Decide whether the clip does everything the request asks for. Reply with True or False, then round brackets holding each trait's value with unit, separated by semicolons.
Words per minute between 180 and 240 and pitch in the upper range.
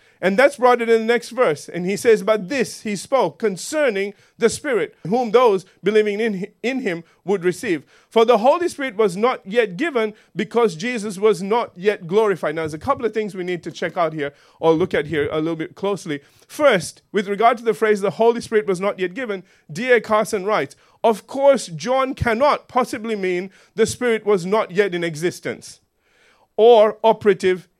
True (195 wpm; 215 Hz)